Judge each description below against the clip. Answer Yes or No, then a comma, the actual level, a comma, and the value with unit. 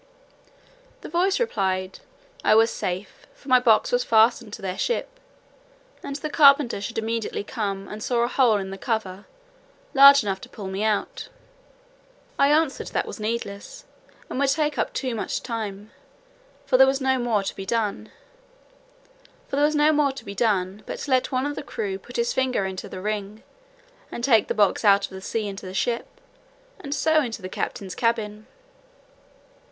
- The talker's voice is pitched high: Yes, high, 230 Hz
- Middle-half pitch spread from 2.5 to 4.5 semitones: No, wide, 5.5 semitones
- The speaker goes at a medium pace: Yes, average, 165 wpm